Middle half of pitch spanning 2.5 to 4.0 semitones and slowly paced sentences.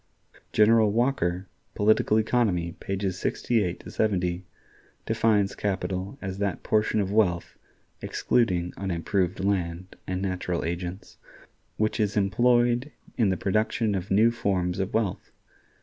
Yes: average, 3.2 semitones; slow, 120 wpm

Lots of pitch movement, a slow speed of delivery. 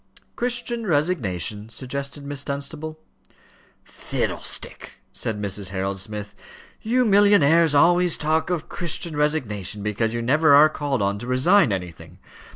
Yes: wide, 7.7 semitones; slow, 125 wpm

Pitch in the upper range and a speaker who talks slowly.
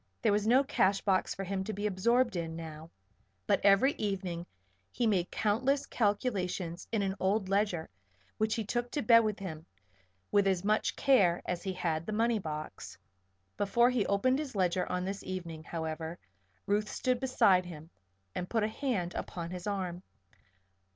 No: high, 195 Hz; average, 170 wpm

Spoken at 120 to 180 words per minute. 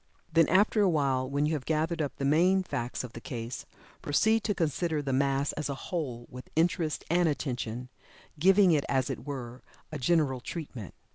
No: average, 190 wpm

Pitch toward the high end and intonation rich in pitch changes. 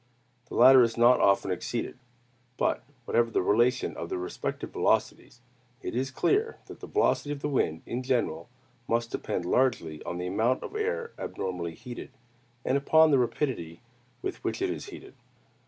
No: low, 120 Hz; wide, 6.3 semitones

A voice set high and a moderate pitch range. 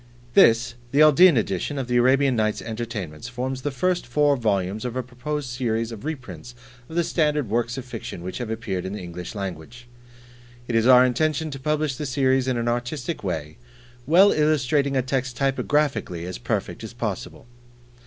No: low, 125 Hz; average, 4.2 semitones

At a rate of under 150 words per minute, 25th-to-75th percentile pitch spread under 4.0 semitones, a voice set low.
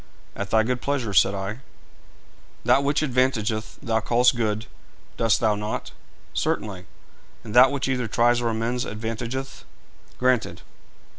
Yes: slow, 135 wpm; average, 2.8 semitones; low, 115 Hz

